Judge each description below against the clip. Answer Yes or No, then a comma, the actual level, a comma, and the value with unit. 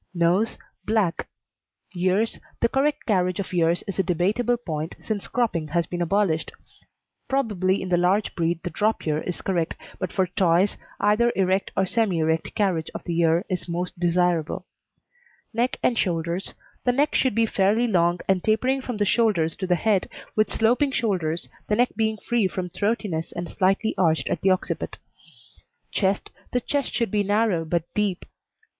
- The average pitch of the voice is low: No, high, 190 Hz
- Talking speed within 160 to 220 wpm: Yes, average, 170 wpm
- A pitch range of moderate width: Yes, average, 4.2 semitones